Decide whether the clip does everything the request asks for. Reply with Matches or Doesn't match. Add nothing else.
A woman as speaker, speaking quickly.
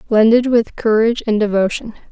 Doesn't match